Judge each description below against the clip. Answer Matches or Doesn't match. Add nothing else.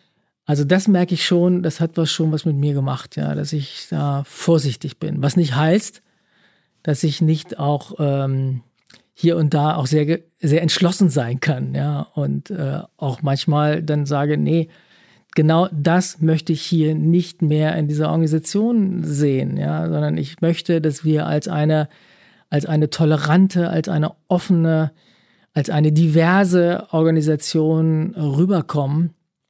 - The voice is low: Doesn't match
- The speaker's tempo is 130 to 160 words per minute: Matches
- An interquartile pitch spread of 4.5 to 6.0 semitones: Doesn't match